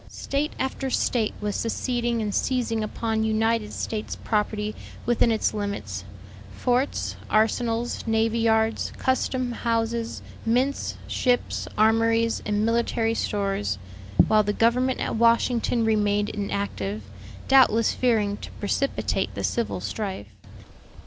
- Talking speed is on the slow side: Yes, slow, 115 wpm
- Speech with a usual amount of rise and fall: No, narrow, 2.1 semitones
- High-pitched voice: Yes, high, 225 Hz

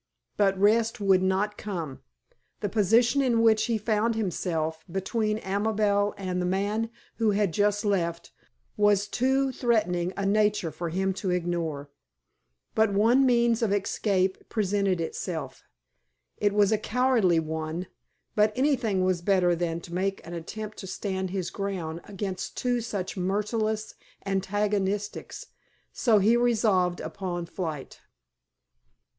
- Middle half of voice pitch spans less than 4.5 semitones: Yes, average, 3.0 semitones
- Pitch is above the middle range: Yes, high, 200 Hz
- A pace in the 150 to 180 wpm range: No, slow, 135 wpm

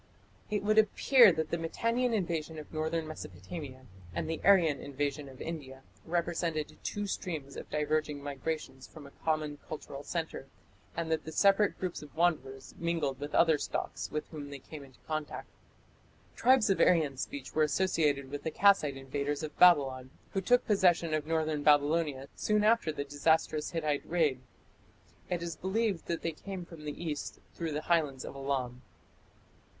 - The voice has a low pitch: No, medium, 155 Hz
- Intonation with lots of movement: No, average, 3.2 semitones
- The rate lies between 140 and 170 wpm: Yes, average, 165 wpm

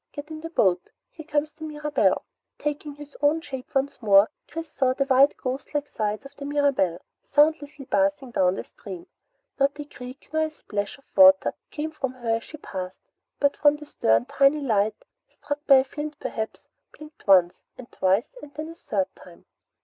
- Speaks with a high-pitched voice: Yes, very high, 280 Hz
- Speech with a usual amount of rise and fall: Yes, average, 4.7 semitones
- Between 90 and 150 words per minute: No, average, 190 wpm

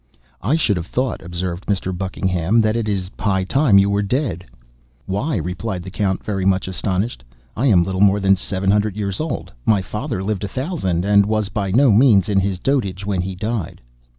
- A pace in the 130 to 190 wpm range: No, average, 200 wpm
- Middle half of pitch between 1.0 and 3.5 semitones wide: Yes, narrow, 2.6 semitones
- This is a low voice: Yes, low, 100 Hz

